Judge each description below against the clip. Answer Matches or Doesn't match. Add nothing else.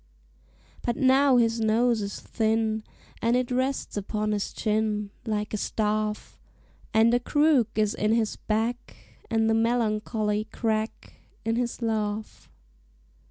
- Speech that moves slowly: Matches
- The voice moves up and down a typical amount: Doesn't match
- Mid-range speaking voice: Doesn't match